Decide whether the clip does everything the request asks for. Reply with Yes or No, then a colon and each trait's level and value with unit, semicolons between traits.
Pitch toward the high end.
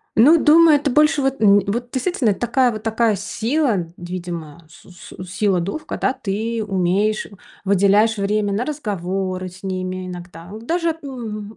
Yes: high, 210 Hz